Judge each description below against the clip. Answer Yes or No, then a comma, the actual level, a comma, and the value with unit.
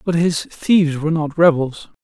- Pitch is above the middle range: No, medium, 160 Hz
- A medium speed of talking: Yes, average, 175 wpm